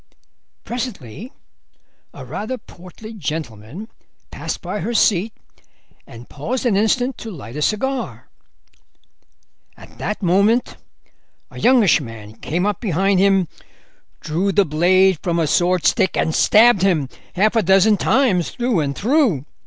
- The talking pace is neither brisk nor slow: No, slow, 130 wpm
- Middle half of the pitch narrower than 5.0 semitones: No, wide, 5.4 semitones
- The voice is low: No, high, 195 Hz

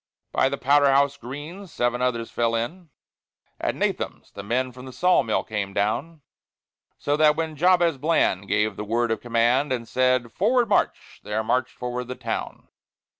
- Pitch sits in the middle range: No, low, 130 Hz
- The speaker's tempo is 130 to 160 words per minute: No, average, 175 wpm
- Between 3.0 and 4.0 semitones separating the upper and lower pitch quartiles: No, average, 4.4 semitones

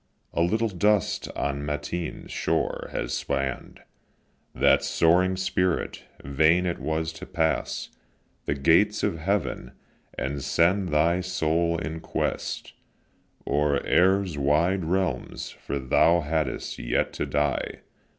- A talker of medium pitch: No, very low, 80 Hz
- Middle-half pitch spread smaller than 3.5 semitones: No, average, 3.8 semitones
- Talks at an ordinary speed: No, slow, 120 wpm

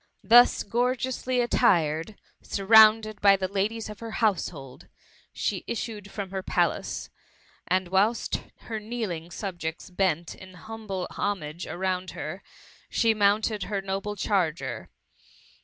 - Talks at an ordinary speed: No, slow, 125 wpm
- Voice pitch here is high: Yes, high, 200 Hz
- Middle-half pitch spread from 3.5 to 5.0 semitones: No, average, 3.1 semitones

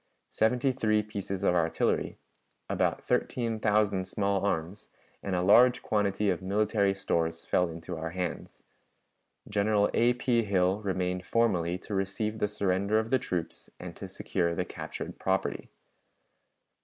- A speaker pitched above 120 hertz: No, low, 100 Hz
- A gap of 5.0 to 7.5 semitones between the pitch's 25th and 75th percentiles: No, average, 2.9 semitones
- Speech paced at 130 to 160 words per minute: Yes, average, 145 wpm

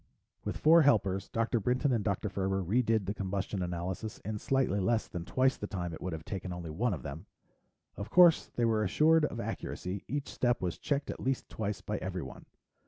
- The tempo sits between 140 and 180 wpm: No, average, 200 wpm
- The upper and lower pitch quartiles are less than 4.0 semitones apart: No, average, 5.0 semitones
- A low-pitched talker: Yes, low, 105 Hz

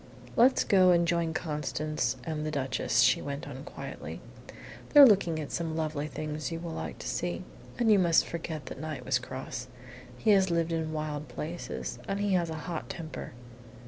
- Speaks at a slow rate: No, average, 185 wpm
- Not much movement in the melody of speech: Yes, narrow, 2.3 semitones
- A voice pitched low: No, medium, 160 Hz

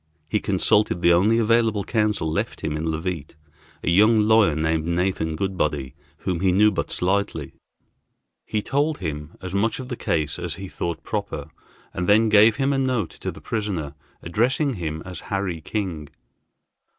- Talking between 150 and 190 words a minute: Yes, average, 165 wpm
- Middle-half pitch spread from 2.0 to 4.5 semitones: No, average, 4.9 semitones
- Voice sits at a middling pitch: No, very low, 95 Hz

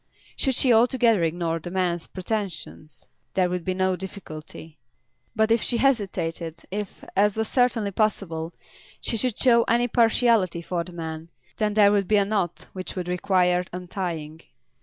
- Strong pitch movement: No, average, 4.2 semitones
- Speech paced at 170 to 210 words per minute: No, average, 160 wpm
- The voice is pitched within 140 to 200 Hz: Yes, high, 190 Hz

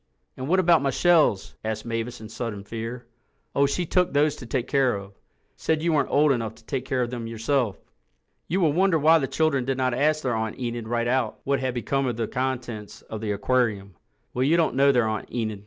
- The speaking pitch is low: Yes, low, 125 Hz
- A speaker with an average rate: No, fast, 225 wpm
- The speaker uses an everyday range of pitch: Yes, average, 3.9 semitones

